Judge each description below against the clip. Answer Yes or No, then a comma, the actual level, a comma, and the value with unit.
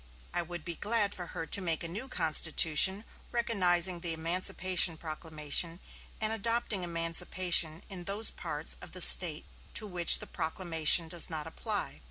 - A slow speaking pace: No, average, 155 wpm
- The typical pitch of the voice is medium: Yes, medium, 175 Hz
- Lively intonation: No, average, 3.0 semitones